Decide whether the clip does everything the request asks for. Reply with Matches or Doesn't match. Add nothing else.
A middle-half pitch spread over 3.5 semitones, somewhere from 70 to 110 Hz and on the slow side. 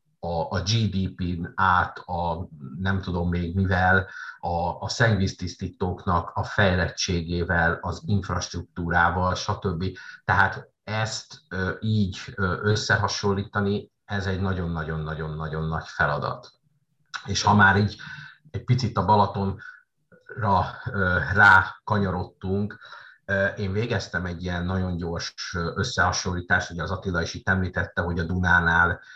Doesn't match